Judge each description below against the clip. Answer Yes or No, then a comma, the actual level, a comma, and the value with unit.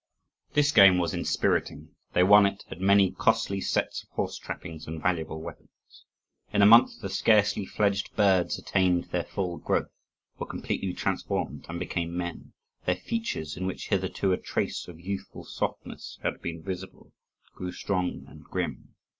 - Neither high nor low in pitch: No, very low, 95 Hz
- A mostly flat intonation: Yes, narrow, 2.3 semitones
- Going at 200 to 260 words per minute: No, average, 160 wpm